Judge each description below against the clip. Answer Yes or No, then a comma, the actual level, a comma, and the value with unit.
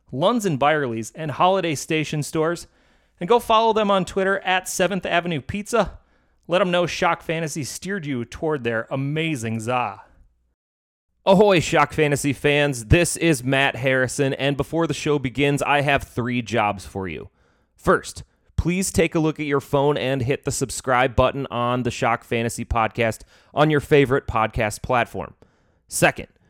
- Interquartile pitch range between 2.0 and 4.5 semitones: No, average, 5.1 semitones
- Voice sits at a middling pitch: Yes, medium, 145 Hz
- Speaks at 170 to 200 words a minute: No, average, 160 wpm